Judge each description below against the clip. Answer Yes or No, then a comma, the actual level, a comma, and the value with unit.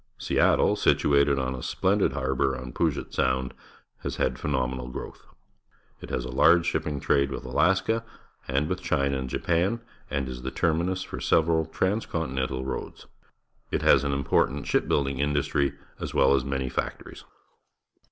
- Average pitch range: Yes, average, 3.9 semitones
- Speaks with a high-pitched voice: No, very low, 70 Hz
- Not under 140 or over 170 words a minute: Yes, average, 160 wpm